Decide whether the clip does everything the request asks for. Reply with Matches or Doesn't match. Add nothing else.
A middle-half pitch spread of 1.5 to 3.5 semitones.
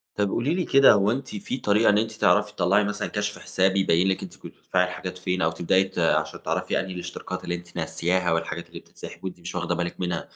Matches